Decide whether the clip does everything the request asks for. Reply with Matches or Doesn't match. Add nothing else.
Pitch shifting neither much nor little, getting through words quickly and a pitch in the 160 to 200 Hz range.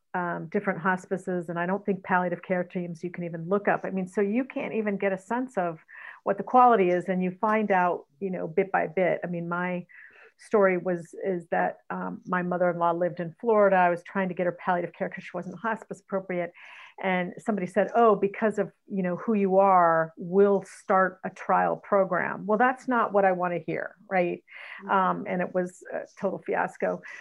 Doesn't match